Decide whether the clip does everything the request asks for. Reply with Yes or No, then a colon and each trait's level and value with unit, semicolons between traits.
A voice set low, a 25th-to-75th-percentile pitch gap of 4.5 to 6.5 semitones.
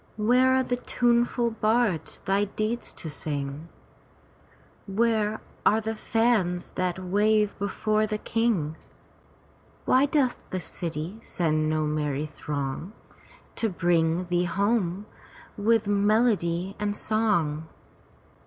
No: high, 205 Hz; average, 4.9 semitones